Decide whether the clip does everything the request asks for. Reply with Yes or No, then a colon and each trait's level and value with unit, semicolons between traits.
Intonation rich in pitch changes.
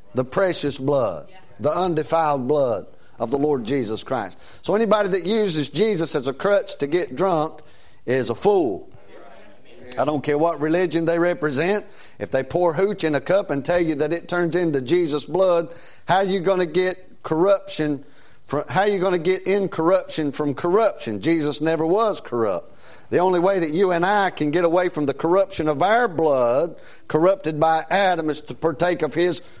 No: average, 4.0 semitones